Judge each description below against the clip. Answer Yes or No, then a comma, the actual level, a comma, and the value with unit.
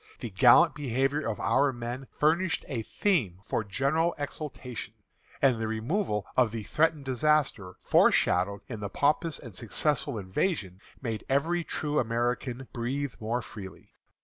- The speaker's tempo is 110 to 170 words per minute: Yes, average, 140 wpm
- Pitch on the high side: No, low, 125 Hz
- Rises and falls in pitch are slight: No, average, 5.0 semitones